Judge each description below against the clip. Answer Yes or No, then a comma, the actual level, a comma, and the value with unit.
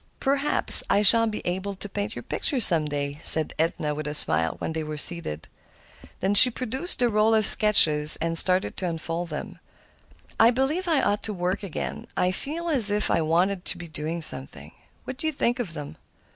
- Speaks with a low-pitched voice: No, medium, 185 Hz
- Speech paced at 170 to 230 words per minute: Yes, average, 200 wpm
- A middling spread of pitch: No, wide, 6.2 semitones